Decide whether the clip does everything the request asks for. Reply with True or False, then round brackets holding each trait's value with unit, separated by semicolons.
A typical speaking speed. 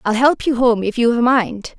False (270 wpm)